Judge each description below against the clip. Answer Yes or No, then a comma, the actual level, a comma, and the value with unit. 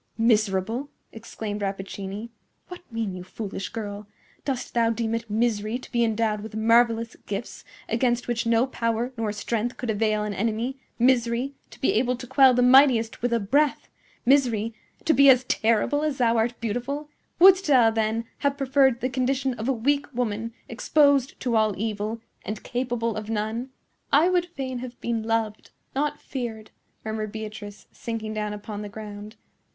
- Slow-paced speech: No, average, 165 wpm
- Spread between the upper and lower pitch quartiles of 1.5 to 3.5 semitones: Yes, average, 2.9 semitones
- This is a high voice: Yes, high, 230 Hz